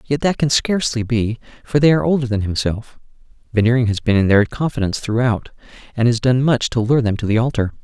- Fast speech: Yes, fast, 215 wpm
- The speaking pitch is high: No, low, 120 Hz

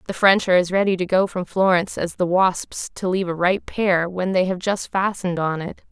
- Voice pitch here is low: No, medium, 185 Hz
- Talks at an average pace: No, fast, 245 wpm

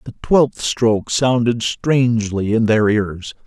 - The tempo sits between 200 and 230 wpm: No, average, 140 wpm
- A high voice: No, low, 115 Hz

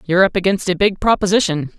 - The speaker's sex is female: Yes, female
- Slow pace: No, average, 200 wpm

